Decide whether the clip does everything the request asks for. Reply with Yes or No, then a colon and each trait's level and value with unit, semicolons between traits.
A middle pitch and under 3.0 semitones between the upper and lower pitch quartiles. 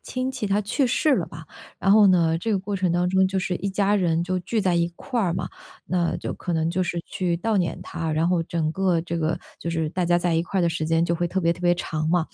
Yes: medium, 175 Hz; narrow, 2.4 semitones